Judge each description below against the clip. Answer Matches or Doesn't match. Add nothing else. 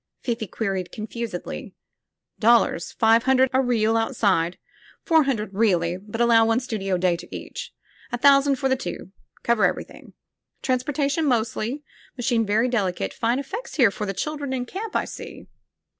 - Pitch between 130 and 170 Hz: Doesn't match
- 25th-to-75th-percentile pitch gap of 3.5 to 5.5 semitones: Matches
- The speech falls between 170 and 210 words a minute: Doesn't match